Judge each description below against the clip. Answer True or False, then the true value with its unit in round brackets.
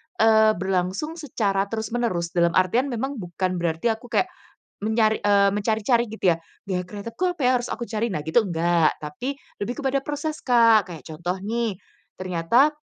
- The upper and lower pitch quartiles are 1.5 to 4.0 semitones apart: False (4.9 semitones)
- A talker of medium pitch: False (215 Hz)